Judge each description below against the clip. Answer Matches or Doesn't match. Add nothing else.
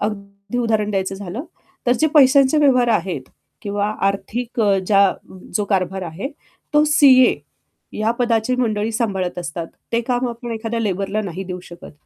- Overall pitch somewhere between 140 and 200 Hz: Doesn't match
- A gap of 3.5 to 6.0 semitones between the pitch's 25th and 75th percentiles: Matches